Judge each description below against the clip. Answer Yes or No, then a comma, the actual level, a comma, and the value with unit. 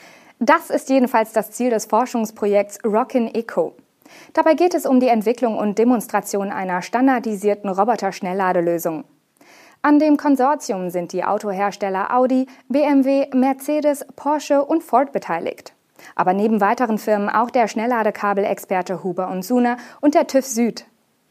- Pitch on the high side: Yes, high, 230 Hz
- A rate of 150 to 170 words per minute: No, average, 130 wpm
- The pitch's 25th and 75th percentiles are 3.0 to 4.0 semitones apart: No, average, 4.9 semitones